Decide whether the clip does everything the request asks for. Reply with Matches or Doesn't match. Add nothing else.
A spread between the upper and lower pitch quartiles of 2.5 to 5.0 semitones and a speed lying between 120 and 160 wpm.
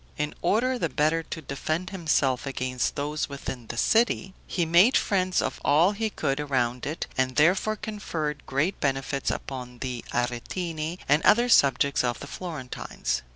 Doesn't match